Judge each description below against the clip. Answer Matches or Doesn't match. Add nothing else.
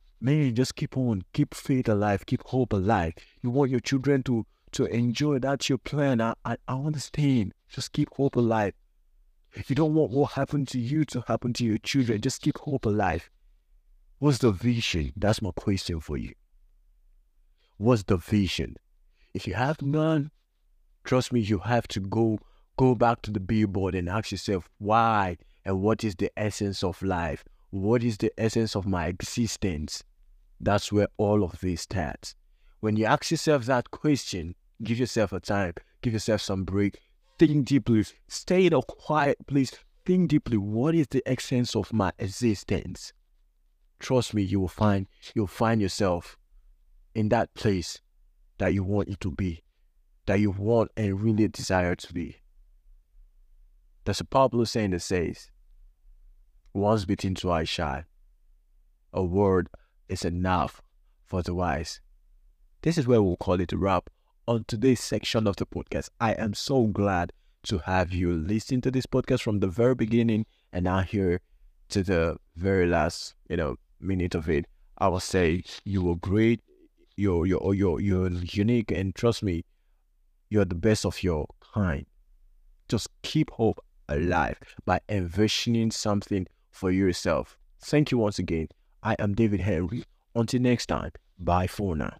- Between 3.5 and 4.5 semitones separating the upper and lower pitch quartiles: Doesn't match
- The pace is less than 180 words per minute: Matches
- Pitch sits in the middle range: Doesn't match